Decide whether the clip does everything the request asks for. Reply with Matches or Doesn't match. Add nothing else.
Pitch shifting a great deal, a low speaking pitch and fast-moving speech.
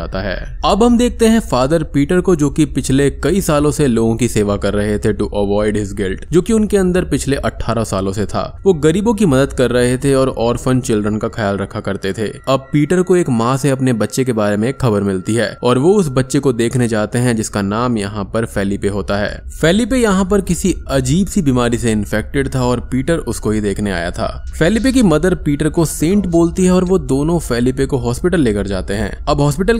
Matches